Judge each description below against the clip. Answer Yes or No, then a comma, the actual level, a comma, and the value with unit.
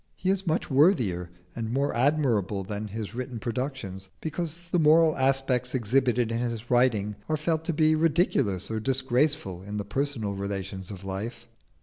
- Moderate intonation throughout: No, wide, 6.2 semitones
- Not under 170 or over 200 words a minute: No, average, 160 wpm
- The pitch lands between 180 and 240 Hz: No, low, 125 Hz